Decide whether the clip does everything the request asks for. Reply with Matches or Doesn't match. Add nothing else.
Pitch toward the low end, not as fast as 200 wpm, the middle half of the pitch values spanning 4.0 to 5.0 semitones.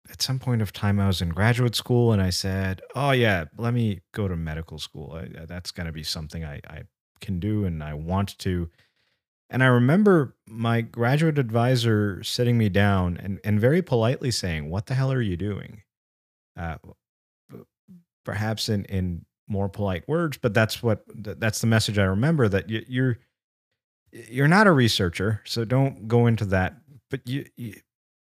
Matches